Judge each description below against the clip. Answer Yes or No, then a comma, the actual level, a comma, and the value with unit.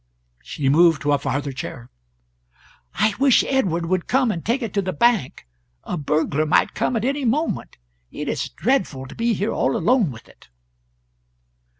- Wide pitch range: Yes, wide, 8.5 semitones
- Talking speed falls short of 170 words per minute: No, average, 175 wpm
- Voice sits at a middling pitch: Yes, medium, 180 Hz